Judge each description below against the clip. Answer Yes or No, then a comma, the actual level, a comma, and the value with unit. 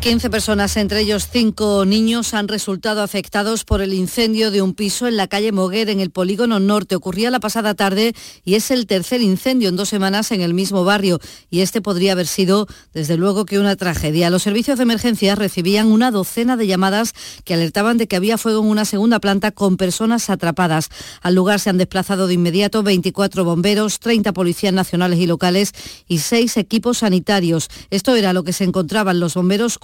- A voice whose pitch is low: No, high, 200 Hz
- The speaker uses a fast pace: Yes, fast, 195 wpm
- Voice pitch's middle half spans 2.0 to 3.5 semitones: Yes, average, 2.7 semitones